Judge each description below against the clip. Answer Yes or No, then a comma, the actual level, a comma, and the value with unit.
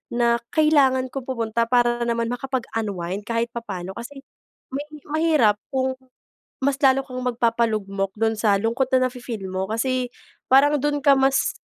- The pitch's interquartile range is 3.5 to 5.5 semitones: No, average, 3.1 semitones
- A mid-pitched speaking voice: No, high, 245 Hz